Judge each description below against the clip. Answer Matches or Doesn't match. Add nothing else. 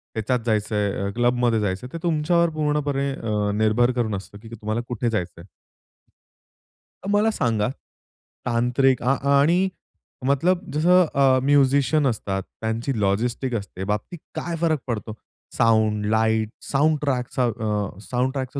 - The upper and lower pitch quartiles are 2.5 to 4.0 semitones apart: Doesn't match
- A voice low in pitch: Matches